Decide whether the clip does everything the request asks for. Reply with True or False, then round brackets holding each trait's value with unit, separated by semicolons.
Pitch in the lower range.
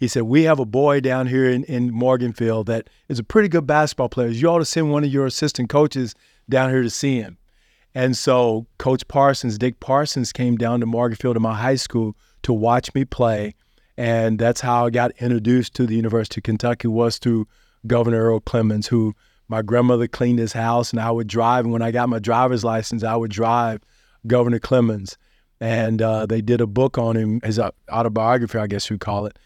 True (120 Hz)